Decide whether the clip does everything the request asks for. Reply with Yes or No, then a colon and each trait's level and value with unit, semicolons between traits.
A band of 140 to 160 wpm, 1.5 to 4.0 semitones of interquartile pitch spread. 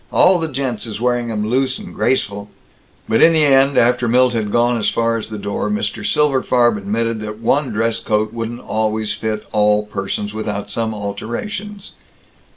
No: average, 175 wpm; average, 3.2 semitones